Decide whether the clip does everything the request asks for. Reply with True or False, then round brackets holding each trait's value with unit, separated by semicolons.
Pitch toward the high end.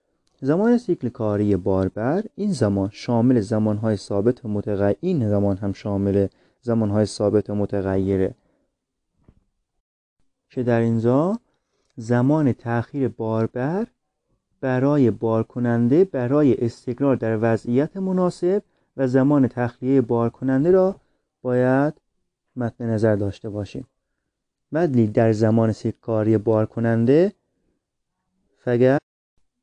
False (120 Hz)